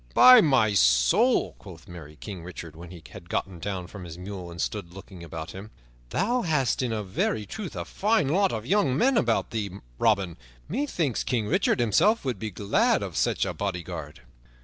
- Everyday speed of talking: Yes, average, 185 wpm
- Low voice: Yes, low, 100 Hz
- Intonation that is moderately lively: No, wide, 7.3 semitones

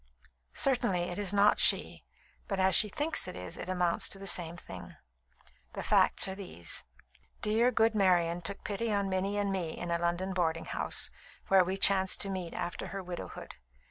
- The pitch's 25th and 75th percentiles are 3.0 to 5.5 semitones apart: No, narrow, 2.5 semitones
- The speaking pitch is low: No, high, 190 Hz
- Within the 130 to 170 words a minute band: No, average, 185 wpm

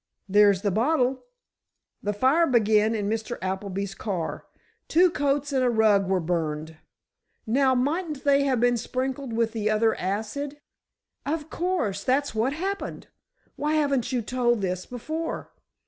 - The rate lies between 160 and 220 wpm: No, average, 140 wpm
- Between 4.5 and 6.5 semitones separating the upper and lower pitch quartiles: Yes, wide, 5.4 semitones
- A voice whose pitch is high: Yes, high, 240 Hz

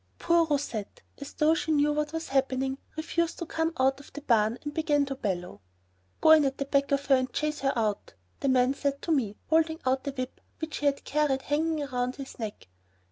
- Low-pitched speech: No, very high, 280 Hz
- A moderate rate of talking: No, fast, 220 wpm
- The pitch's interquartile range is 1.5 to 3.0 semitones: Yes, narrow, 2.6 semitones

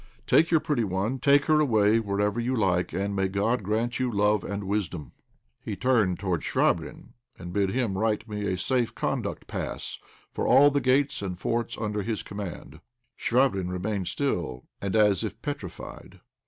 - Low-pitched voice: Yes, low, 105 Hz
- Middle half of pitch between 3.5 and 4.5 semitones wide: Yes, average, 3.9 semitones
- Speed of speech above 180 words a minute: No, average, 170 wpm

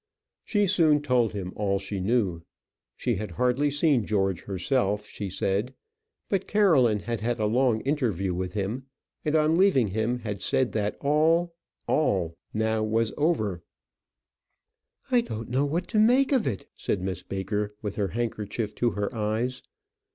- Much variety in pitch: Yes, wide, 6.0 semitones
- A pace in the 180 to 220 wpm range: No, average, 160 wpm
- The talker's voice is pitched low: Yes, low, 115 Hz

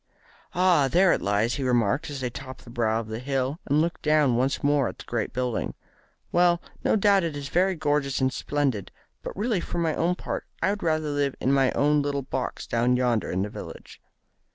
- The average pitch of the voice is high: No, medium, 140 Hz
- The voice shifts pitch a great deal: No, average, 4.4 semitones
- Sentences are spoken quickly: Yes, fast, 215 wpm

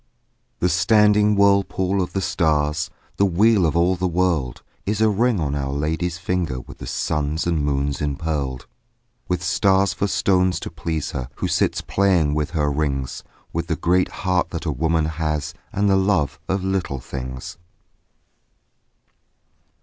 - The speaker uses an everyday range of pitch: Yes, average, 4.3 semitones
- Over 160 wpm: No, average, 155 wpm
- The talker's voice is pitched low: Yes, very low, 85 Hz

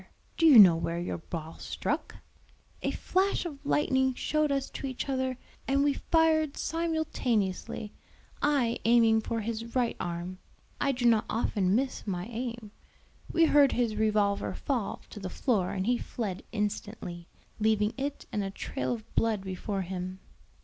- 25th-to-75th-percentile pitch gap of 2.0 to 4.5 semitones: No, wide, 5.5 semitones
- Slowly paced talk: No, average, 155 wpm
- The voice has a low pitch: No, high, 230 Hz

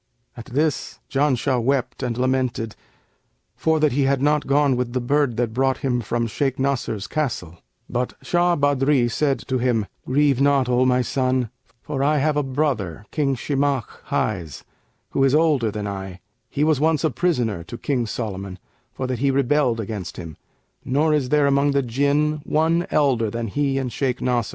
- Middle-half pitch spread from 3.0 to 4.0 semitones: Yes, average, 3.4 semitones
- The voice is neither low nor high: No, low, 130 Hz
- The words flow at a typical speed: Yes, average, 180 wpm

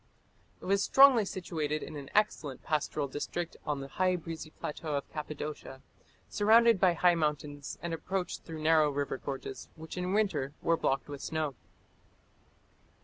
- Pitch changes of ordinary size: Yes, average, 3.8 semitones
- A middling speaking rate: Yes, average, 150 wpm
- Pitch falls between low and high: Yes, medium, 155 Hz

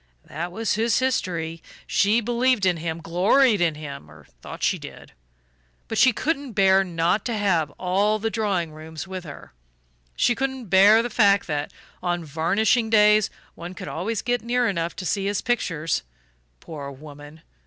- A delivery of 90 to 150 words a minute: No, average, 165 wpm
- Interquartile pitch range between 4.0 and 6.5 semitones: Yes, average, 5.3 semitones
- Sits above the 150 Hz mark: Yes, high, 190 Hz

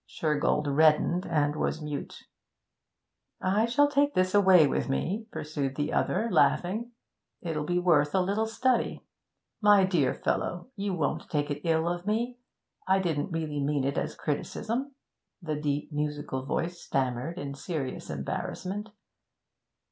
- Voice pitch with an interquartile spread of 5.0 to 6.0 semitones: Yes, wide, 5.4 semitones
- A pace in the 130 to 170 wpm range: Yes, average, 145 wpm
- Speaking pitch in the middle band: Yes, medium, 165 Hz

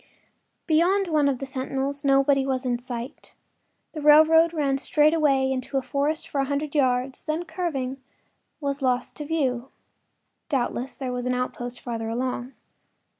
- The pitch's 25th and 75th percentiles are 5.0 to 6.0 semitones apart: No, average, 2.9 semitones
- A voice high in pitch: Yes, very high, 275 Hz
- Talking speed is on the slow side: No, average, 155 wpm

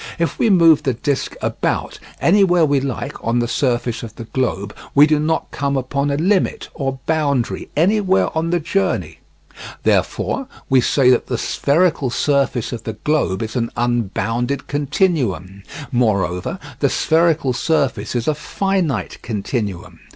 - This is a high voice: No, medium, 140 Hz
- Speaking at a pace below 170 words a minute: Yes, average, 150 wpm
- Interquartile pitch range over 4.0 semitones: Yes, average, 5.1 semitones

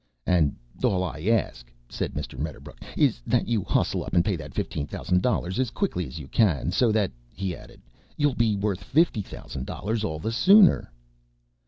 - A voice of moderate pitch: No, very low, 95 Hz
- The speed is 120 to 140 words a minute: No, average, 185 wpm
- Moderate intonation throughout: No, wide, 6.4 semitones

